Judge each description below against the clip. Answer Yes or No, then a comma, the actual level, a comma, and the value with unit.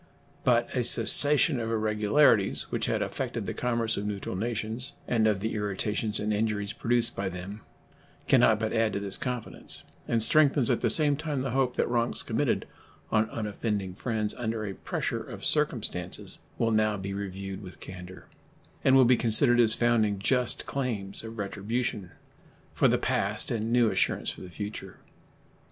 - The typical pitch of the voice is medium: No, low, 110 Hz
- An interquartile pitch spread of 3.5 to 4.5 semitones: No, average, 2.9 semitones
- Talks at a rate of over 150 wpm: Yes, average, 170 wpm